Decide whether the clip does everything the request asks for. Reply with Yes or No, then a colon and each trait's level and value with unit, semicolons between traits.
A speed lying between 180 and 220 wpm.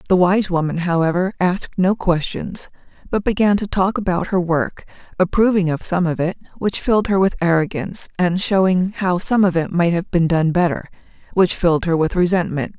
Yes: average, 190 wpm